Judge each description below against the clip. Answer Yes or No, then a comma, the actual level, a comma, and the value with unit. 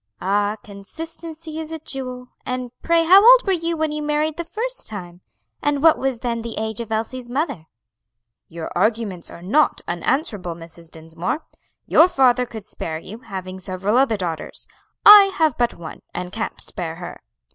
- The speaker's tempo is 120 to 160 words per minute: No, average, 170 wpm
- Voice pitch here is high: Yes, high, 235 Hz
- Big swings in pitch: Yes, wide, 8.8 semitones